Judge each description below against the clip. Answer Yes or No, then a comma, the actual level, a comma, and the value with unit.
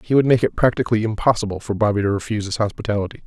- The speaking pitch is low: Yes, low, 105 Hz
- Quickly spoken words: Yes, fast, 220 wpm